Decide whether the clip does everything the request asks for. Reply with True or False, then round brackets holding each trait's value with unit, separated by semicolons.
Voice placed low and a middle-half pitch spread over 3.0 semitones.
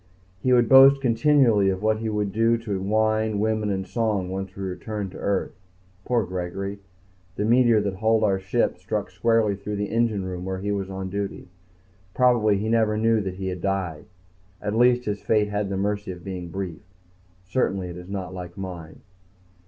False (100 Hz; 2.6 semitones)